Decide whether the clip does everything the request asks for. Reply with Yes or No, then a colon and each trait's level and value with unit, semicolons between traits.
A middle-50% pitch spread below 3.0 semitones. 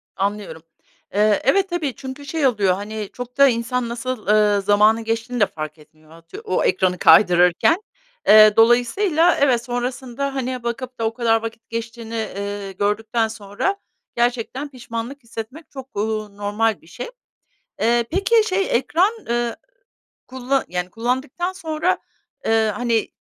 No: average, 3.8 semitones